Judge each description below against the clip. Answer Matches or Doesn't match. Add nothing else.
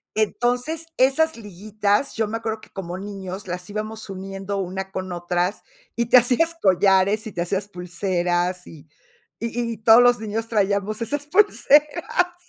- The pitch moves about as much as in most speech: Matches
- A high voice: Matches